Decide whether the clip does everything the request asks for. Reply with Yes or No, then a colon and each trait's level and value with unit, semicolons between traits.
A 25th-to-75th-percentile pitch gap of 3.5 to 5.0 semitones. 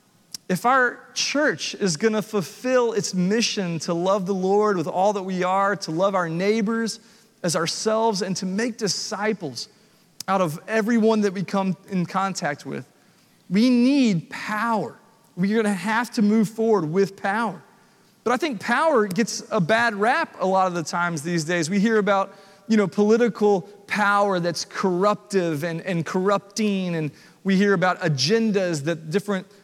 No: average, 3.0 semitones